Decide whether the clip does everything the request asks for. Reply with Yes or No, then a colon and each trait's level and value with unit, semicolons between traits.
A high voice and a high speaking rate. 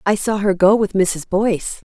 Yes: high, 200 Hz; fast, 220 wpm